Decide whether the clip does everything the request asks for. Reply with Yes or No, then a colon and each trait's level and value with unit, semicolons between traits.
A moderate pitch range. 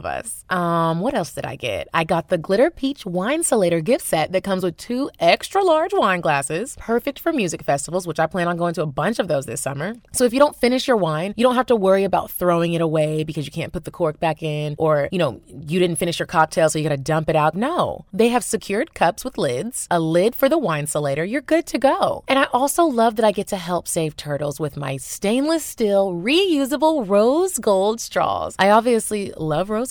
No: wide, 7.6 semitones